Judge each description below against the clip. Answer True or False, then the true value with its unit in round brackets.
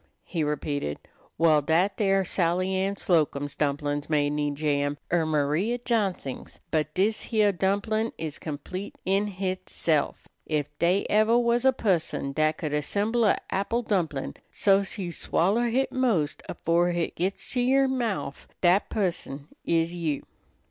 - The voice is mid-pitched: True (175 Hz)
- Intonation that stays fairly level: False (5.4 semitones)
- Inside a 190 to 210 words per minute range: False (145 wpm)